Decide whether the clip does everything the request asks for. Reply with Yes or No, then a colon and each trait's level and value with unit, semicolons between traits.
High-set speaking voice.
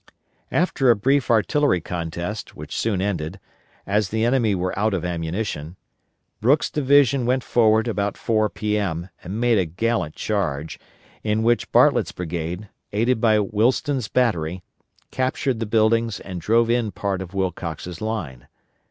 No: low, 105 Hz